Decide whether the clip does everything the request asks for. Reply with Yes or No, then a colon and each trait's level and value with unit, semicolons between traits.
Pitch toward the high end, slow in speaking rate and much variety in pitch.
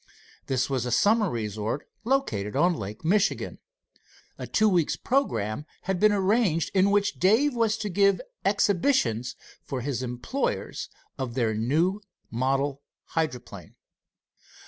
No: medium, 165 Hz; slow, 125 wpm; wide, 8.8 semitones